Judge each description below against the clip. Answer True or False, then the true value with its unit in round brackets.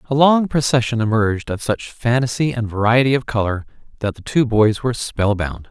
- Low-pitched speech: True (120 Hz)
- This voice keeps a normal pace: True (180 wpm)